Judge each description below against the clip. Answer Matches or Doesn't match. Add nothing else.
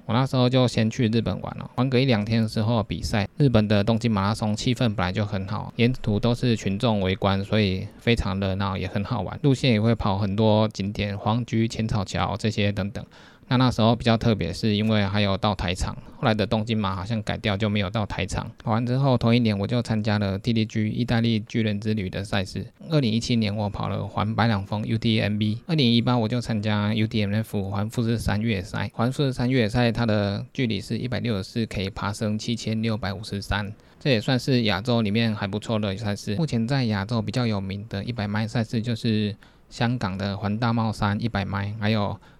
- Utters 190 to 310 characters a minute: Doesn't match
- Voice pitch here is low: Matches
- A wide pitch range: Doesn't match